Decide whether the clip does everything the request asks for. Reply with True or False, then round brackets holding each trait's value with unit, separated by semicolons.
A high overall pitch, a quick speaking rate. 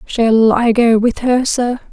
False (235 Hz; 190 wpm)